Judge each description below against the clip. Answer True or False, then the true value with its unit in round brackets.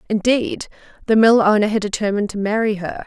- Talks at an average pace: True (175 wpm)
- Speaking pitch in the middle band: False (215 Hz)